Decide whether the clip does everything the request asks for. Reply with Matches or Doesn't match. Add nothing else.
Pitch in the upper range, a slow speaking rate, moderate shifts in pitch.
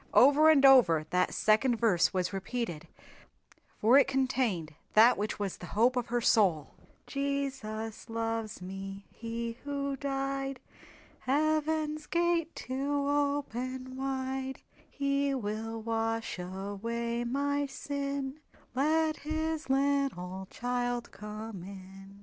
Matches